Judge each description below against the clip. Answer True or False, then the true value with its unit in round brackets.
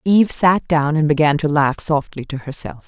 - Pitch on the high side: False (150 Hz)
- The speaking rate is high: True (210 wpm)